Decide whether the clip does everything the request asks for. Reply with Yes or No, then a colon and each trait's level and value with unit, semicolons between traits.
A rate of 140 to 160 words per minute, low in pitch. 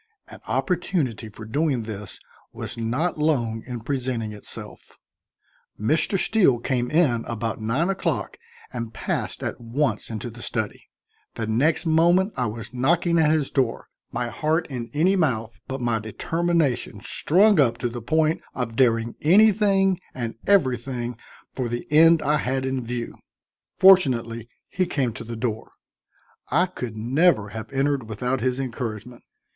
Yes: average, 150 wpm; low, 125 Hz